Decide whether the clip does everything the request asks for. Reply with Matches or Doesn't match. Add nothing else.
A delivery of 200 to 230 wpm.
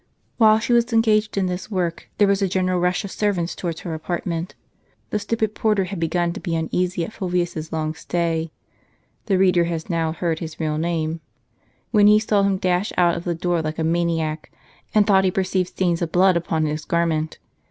Matches